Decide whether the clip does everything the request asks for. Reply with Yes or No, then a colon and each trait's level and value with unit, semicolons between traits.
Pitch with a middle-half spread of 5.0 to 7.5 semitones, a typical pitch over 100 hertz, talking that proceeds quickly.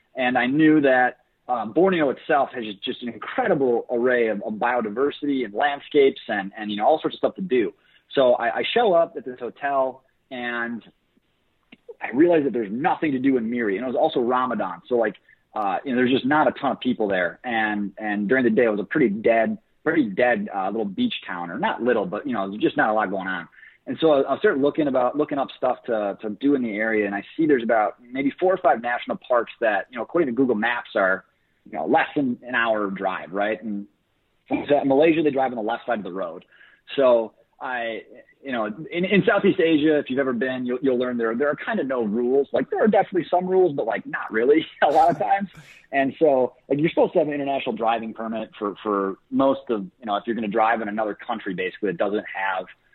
Yes: wide, 5.5 semitones; low, 125 Hz; fast, 240 wpm